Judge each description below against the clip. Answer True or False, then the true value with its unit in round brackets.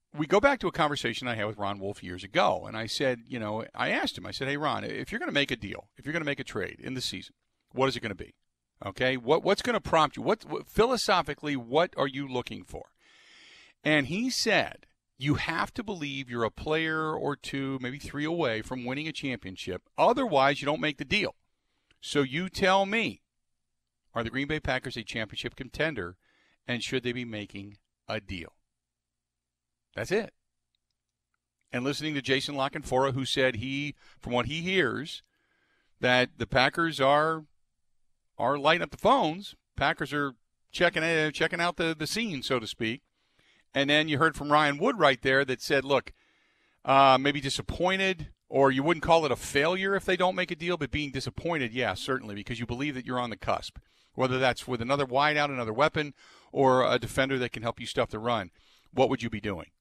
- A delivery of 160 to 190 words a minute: False (205 wpm)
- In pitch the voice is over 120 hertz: True (135 Hz)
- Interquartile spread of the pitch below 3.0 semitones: False (4.4 semitones)